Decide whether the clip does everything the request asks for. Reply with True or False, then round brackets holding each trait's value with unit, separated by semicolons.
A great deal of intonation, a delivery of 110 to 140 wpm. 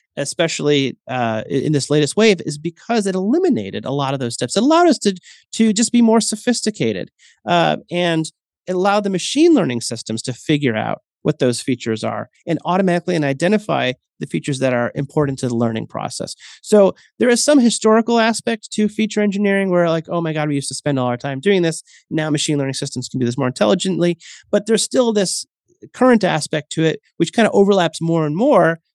False (7.1 semitones; 205 wpm)